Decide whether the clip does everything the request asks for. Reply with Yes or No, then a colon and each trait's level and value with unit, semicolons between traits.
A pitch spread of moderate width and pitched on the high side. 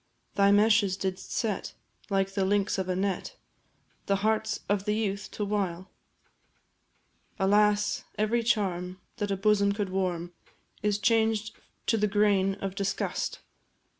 No: narrow, 1.6 semitones; high, 200 Hz